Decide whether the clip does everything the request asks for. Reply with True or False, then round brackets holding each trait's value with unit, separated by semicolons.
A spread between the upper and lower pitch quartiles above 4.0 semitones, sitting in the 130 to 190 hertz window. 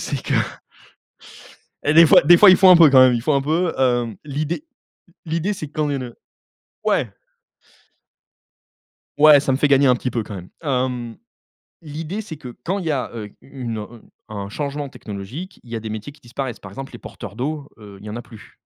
True (4.7 semitones; 135 Hz)